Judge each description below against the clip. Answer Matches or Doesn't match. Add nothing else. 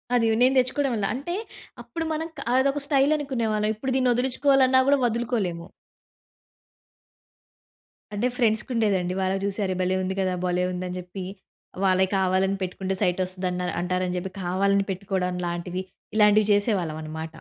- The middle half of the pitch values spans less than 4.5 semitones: Doesn't match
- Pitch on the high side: Matches